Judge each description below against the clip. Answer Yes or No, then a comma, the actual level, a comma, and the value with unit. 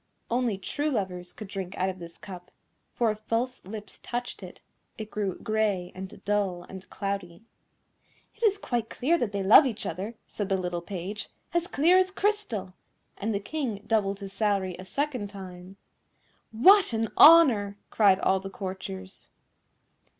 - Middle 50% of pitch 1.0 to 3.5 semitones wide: No, average, 4.0 semitones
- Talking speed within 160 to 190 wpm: Yes, average, 165 wpm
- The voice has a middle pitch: No, high, 205 Hz